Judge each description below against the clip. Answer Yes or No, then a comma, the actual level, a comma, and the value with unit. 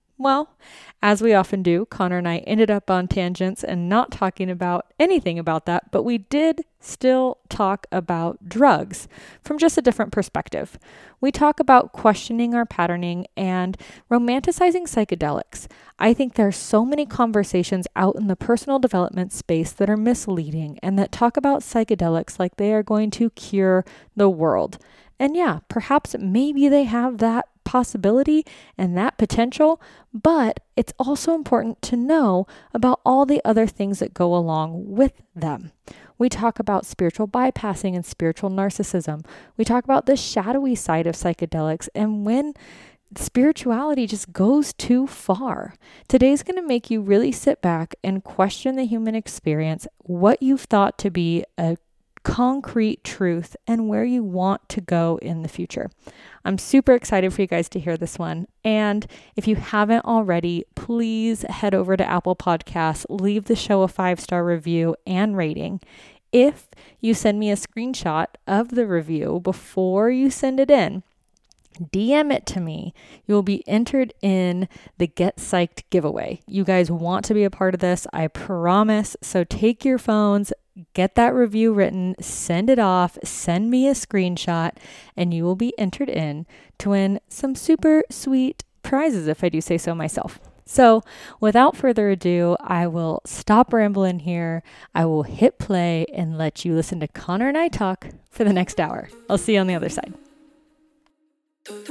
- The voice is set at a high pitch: Yes, high, 205 Hz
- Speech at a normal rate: Yes, average, 165 wpm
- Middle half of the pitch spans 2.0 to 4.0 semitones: No, wide, 5.5 semitones